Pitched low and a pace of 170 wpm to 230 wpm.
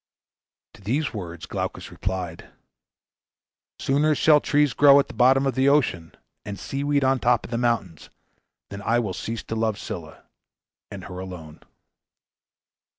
No: low, 115 Hz; average, 155 wpm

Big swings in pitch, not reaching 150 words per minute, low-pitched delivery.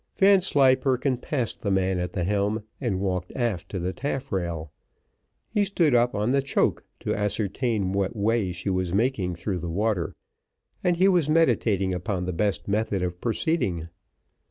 No: wide, 5.9 semitones; average, 160 wpm; low, 105 Hz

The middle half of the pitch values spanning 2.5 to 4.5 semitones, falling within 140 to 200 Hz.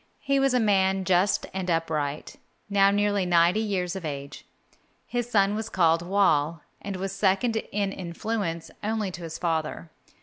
Yes: average, 3.5 semitones; high, 190 Hz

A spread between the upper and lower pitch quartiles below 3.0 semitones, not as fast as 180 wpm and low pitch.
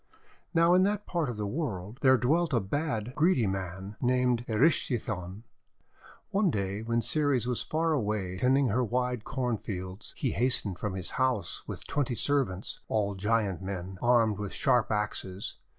No: average, 4.8 semitones; average, 160 wpm; low, 115 Hz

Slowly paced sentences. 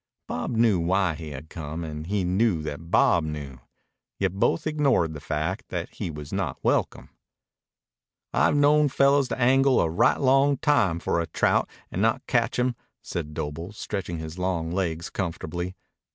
No: average, 165 wpm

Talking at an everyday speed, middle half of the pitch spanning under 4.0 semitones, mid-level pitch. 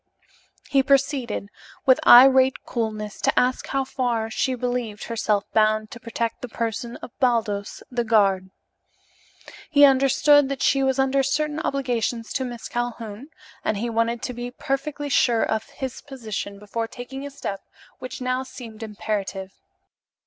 No: average, 150 wpm; average, 3.3 semitones; high, 240 Hz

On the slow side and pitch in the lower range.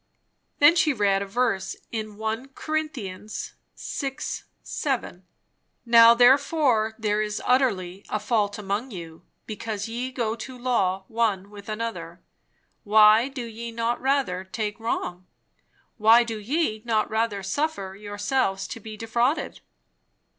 No: slow, 130 wpm; high, 220 Hz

